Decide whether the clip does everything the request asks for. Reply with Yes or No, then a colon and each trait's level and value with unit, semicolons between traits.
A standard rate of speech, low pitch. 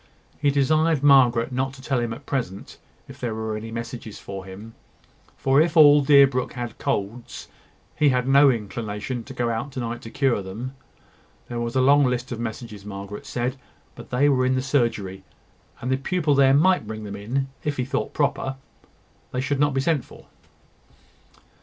Yes: average, 185 wpm; low, 125 Hz